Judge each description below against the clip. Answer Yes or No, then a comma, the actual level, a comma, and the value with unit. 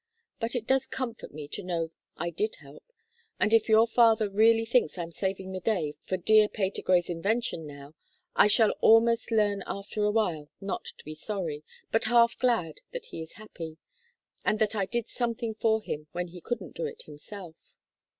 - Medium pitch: No, high, 210 Hz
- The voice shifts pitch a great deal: No, average, 4.8 semitones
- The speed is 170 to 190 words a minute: Yes, average, 185 wpm